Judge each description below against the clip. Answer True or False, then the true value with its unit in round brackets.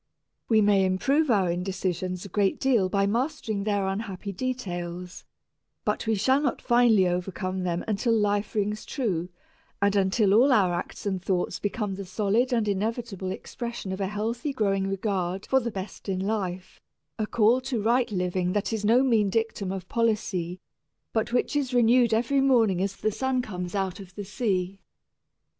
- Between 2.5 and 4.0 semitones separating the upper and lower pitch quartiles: True (3.6 semitones)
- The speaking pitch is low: False (205 Hz)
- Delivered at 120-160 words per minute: False (170 wpm)